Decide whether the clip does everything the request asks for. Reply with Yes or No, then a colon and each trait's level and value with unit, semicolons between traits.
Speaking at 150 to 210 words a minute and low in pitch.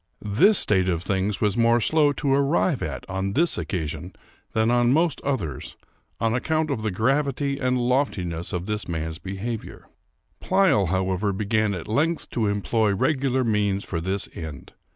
Yes: average, 160 wpm; low, 110 Hz